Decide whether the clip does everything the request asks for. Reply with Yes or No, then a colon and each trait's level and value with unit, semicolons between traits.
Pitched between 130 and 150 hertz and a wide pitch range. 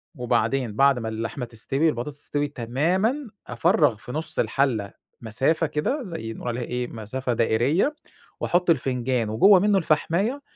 Yes: low, 135 Hz; wide, 5.8 semitones